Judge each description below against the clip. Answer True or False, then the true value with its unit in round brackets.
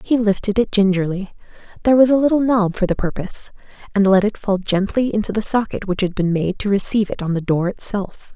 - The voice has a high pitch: True (205 Hz)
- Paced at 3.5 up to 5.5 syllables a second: False (6.0 syllables/s)